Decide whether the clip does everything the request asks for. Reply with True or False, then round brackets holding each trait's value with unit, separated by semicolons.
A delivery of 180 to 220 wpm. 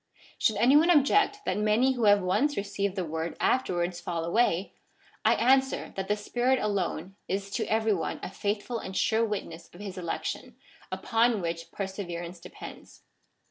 False (165 wpm)